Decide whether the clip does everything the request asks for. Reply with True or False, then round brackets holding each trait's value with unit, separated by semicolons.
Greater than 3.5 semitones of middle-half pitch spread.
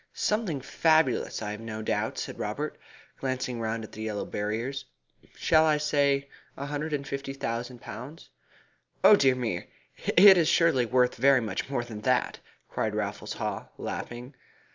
True (4.1 semitones)